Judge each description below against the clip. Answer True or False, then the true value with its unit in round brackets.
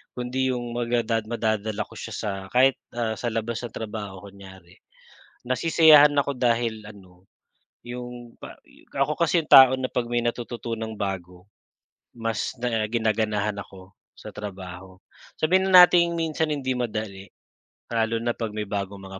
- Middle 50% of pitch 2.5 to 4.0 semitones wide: True (3.6 semitones)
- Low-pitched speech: True (115 Hz)